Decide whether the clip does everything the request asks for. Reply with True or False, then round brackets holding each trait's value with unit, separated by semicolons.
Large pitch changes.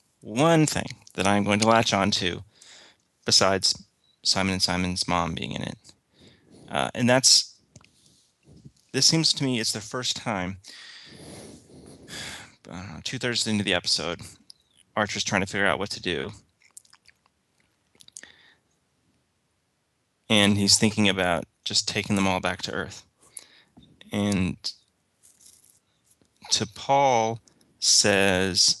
False (3.6 semitones)